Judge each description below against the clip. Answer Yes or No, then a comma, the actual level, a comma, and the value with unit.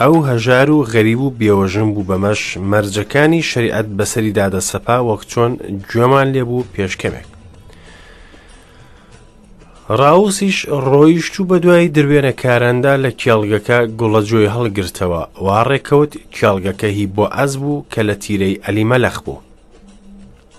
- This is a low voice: Yes, low, 115 Hz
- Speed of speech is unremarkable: No, slow, 110 wpm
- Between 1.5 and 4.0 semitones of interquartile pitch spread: No, wide, 5.4 semitones